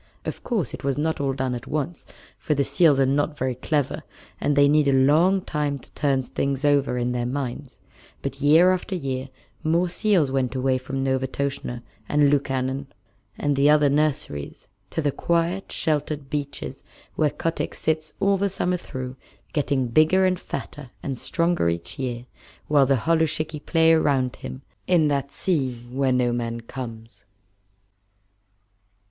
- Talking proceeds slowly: No, average, 160 wpm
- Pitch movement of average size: Yes, average, 3.1 semitones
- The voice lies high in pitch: No, medium, 140 Hz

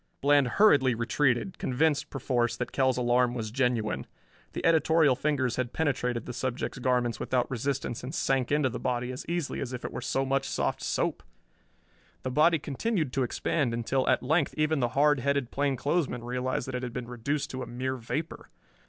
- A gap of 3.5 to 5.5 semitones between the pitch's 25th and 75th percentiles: No, average, 2.7 semitones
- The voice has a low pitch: Yes, low, 130 Hz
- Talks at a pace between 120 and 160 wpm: No, average, 185 wpm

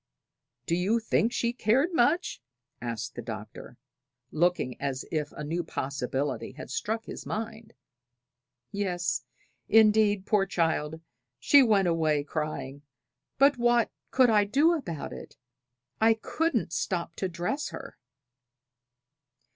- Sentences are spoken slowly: Yes, slow, 125 wpm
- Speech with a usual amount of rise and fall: No, wide, 7.0 semitones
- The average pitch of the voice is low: No, medium, 185 Hz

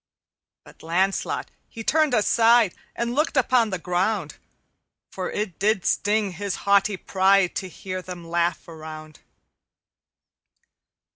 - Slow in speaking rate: Yes, slow, 120 wpm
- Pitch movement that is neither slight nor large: Yes, average, 3.7 semitones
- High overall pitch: Yes, high, 195 Hz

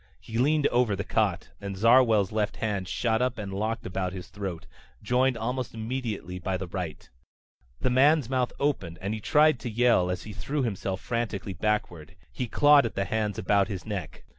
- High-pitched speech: No, low, 110 Hz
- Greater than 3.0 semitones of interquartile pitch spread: Yes, average, 4.5 semitones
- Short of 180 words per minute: No, average, 190 wpm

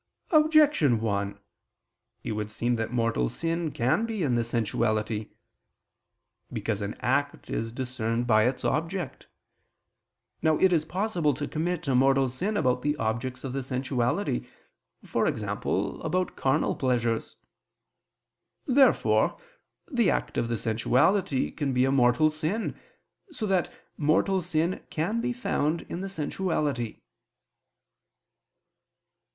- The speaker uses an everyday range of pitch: No, wide, 6.7 semitones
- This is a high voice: No, low, 135 Hz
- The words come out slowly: Yes, slow, 125 wpm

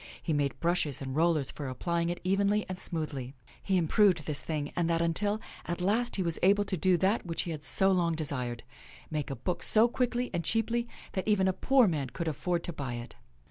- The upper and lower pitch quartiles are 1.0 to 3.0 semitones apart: No, average, 4.4 semitones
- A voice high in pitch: No, medium, 170 Hz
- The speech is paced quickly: Yes, fast, 225 wpm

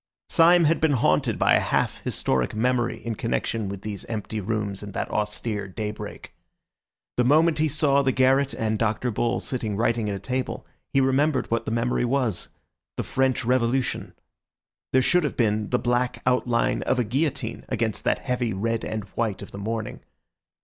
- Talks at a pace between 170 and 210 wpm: Yes, average, 175 wpm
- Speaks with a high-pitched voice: No, low, 120 Hz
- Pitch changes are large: No, average, 3.4 semitones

